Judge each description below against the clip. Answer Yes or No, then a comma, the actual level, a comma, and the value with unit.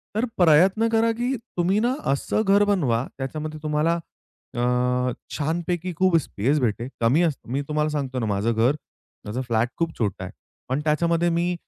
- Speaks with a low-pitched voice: No, medium, 150 Hz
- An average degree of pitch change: No, wide, 5.8 semitones